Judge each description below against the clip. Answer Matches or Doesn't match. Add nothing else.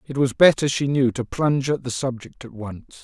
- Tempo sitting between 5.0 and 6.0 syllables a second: Matches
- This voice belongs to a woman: Doesn't match